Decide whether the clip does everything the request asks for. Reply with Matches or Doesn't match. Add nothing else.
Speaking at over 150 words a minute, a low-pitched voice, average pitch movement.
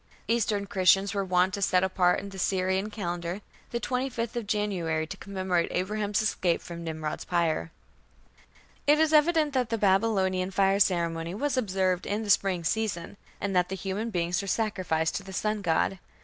Doesn't match